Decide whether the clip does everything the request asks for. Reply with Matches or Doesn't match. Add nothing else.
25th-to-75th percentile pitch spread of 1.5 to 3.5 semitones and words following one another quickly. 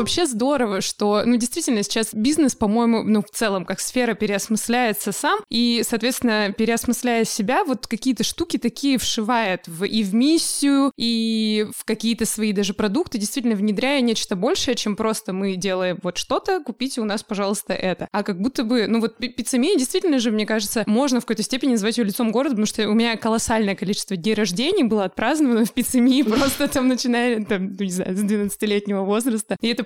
Matches